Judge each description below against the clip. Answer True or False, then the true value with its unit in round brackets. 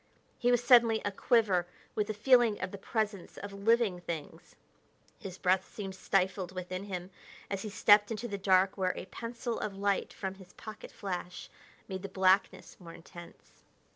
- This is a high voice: True (195 Hz)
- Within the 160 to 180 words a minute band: True (170 wpm)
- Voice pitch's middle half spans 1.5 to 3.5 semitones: True (2.6 semitones)